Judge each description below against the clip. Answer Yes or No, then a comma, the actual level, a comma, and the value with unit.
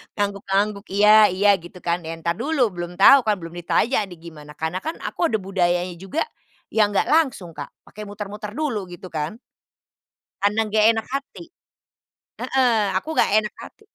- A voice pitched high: Yes, high, 200 Hz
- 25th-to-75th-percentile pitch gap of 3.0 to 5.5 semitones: Yes, average, 3.9 semitones